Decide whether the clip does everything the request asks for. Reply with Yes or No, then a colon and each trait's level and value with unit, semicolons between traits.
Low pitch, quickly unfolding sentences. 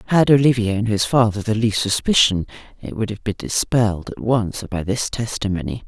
No: low, 115 Hz; average, 185 wpm